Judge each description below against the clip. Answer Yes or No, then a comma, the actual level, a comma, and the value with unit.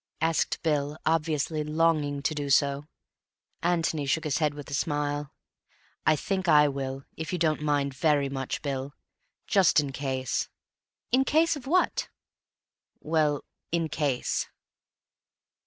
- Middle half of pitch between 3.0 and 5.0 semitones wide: No, narrow, 2.4 semitones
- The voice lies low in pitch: No, medium, 150 Hz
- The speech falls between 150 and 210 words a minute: No, slow, 135 wpm